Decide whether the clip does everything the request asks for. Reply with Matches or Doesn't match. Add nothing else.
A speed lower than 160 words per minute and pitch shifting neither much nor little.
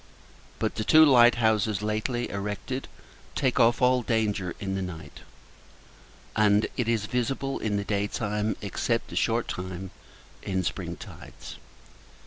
Matches